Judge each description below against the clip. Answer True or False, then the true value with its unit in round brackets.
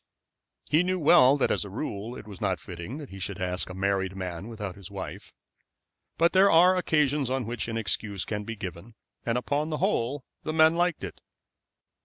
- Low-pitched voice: True (115 Hz)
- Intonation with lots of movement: True (7.7 semitones)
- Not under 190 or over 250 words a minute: True (200 wpm)